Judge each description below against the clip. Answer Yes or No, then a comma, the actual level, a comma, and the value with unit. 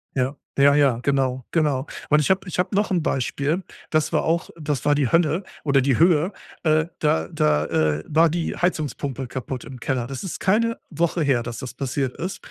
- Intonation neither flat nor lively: Yes, average, 4.2 semitones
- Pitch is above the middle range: No, medium, 145 Hz